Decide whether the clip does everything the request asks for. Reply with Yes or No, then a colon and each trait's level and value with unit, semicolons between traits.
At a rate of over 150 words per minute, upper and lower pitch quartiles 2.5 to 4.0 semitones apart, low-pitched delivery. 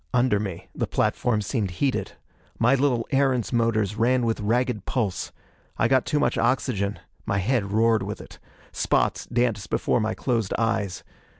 Yes: average, 160 wpm; average, 3.3 semitones; low, 115 Hz